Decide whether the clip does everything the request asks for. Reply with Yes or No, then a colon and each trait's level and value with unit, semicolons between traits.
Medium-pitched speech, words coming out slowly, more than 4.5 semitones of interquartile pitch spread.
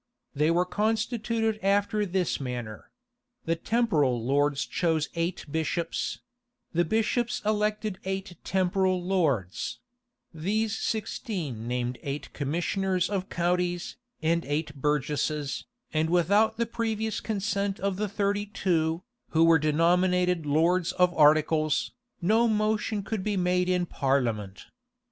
Yes: medium, 180 Hz; slow, 120 wpm; average, 4.9 semitones